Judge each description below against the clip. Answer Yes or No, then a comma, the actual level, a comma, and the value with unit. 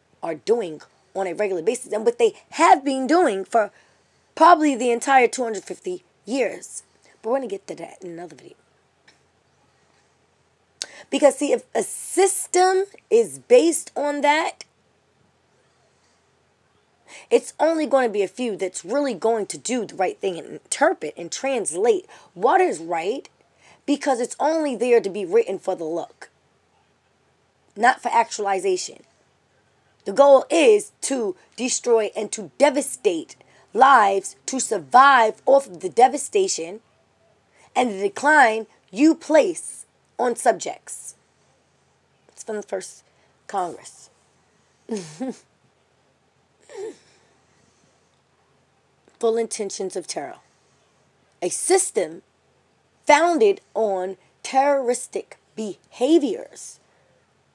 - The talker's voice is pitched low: No, very high, 265 Hz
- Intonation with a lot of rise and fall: Yes, wide, 8.0 semitones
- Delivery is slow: Yes, slow, 110 wpm